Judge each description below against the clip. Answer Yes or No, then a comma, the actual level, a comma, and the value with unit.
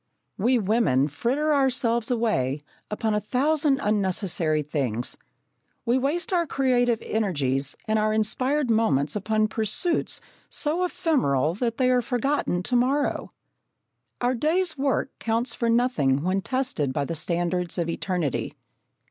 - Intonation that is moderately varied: No, wide, 7.0 semitones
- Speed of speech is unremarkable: No, slow, 130 wpm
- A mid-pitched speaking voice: No, high, 225 Hz